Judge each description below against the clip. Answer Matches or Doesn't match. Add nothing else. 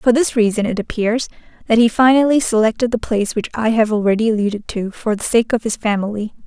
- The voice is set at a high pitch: Matches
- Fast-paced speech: Matches